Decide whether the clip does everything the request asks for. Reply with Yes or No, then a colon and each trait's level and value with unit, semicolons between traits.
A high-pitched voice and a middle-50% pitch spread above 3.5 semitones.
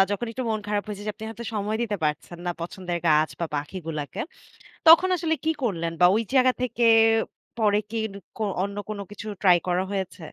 Yes: high, 205 Hz; average, 4.3 semitones